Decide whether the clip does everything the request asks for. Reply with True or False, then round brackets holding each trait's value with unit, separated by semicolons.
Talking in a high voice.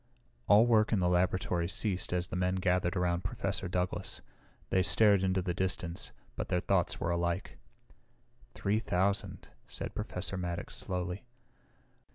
False (90 Hz)